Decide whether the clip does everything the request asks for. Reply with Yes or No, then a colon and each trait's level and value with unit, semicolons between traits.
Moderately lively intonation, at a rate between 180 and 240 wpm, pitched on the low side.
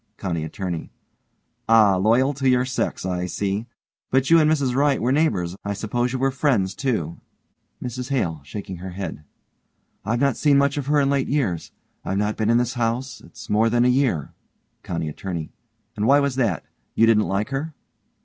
No: wide, 5.9 semitones; average, 190 wpm; low, 115 Hz